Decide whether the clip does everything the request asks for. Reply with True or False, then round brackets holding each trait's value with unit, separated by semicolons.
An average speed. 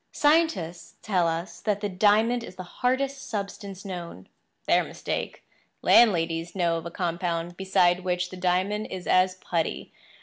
True (145 wpm)